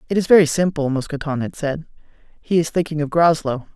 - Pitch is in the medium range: Yes, medium, 155 Hz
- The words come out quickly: No, average, 190 wpm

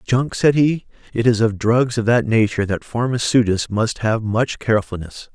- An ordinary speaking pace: Yes, average, 180 wpm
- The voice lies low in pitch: Yes, low, 115 Hz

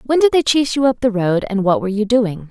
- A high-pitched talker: Yes, high, 230 Hz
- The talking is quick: Yes, fast, 310 wpm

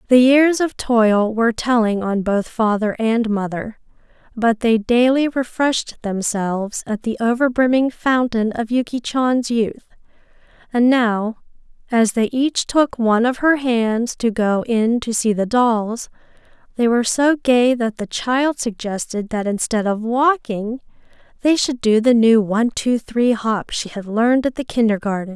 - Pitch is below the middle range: No, high, 235 Hz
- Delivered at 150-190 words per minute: Yes, average, 160 wpm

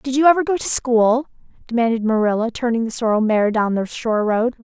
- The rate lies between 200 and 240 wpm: Yes, fast, 205 wpm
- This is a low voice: No, high, 235 Hz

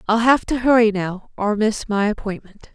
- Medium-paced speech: Yes, average, 195 wpm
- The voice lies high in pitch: Yes, high, 215 Hz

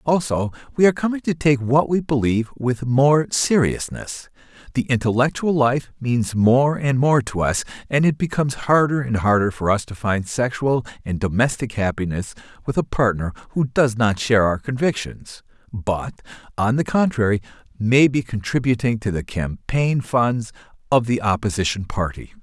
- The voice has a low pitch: Yes, low, 125 Hz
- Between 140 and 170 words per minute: Yes, average, 160 wpm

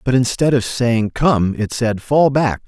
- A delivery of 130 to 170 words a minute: No, average, 200 wpm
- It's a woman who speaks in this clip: No, male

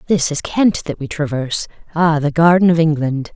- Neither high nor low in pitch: Yes, medium, 160 Hz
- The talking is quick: No, average, 195 wpm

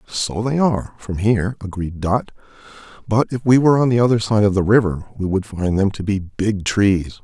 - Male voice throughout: Yes, male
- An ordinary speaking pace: No, fast, 215 wpm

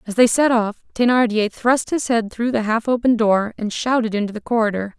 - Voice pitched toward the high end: Yes, high, 225 Hz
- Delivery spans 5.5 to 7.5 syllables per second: No, 5.3 syllables/s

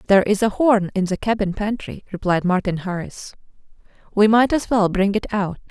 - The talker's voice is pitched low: No, high, 205 Hz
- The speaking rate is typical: Yes, average, 190 wpm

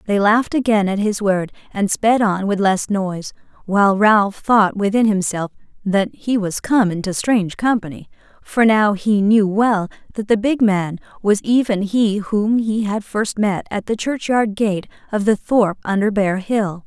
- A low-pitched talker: No, high, 205 Hz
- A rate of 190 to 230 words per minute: No, average, 180 wpm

